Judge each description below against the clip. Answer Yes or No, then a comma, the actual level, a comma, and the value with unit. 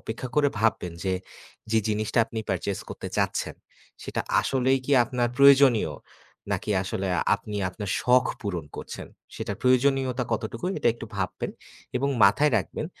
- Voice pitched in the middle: No, low, 120 Hz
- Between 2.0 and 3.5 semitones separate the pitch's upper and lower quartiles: No, average, 4.2 semitones